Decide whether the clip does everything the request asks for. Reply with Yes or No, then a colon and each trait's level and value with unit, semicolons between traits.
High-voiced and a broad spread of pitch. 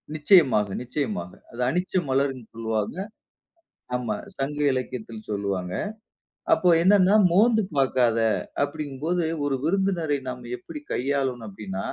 No: low, 135 Hz; wide, 6.2 semitones